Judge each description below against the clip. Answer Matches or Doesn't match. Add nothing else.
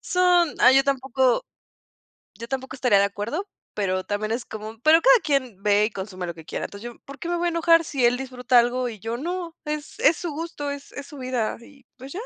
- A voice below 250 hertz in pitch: Doesn't match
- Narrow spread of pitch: Doesn't match